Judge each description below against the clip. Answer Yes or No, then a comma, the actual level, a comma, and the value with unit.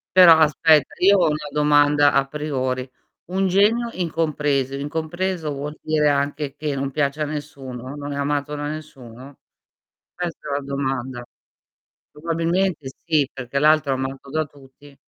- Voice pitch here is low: No, medium, 145 Hz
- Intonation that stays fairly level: Yes, narrow, 2.3 semitones